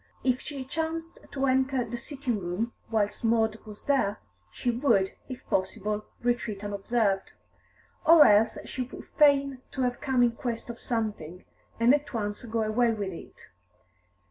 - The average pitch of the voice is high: Yes, high, 235 Hz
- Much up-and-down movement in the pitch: No, average, 3.8 semitones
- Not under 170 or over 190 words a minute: No, average, 155 wpm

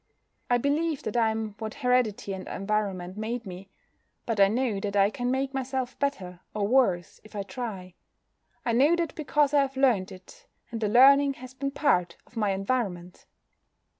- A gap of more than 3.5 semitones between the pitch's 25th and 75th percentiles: Yes, average, 5.2 semitones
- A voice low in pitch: No, high, 230 Hz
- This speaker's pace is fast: No, average, 180 wpm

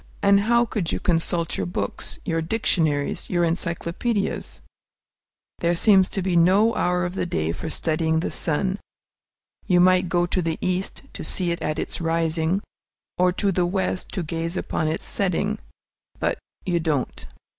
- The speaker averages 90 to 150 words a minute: No, average, 165 wpm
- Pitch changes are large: No, narrow, 2.6 semitones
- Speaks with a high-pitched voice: No, medium, 175 Hz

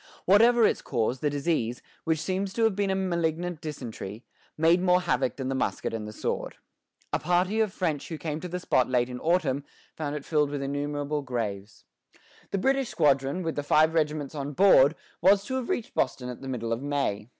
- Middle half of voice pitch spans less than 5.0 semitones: No, average, 5.3 semitones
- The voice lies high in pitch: No, medium, 150 Hz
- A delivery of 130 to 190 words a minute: No, fast, 205 wpm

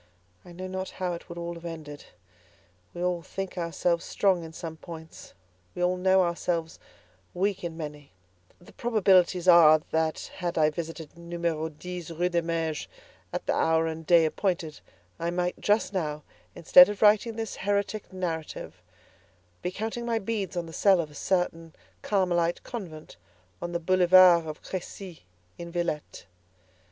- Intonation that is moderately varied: No, narrow, 2.3 semitones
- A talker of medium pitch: Yes, medium, 175 Hz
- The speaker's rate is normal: Yes, average, 160 wpm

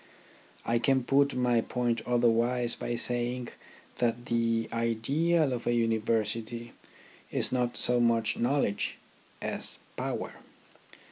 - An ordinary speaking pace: No, slow, 115 wpm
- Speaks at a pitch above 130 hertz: No, low, 120 Hz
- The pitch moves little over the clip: Yes, narrow, 1.3 semitones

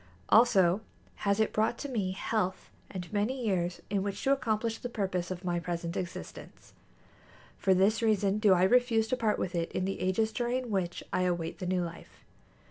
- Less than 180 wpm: No, average, 190 wpm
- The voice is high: Yes, high, 195 Hz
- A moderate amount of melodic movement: Yes, average, 3.6 semitones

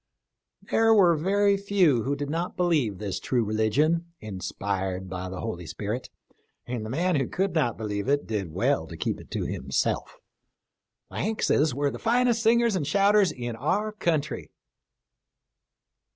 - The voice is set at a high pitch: No, medium, 145 Hz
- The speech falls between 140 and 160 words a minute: Yes, average, 155 wpm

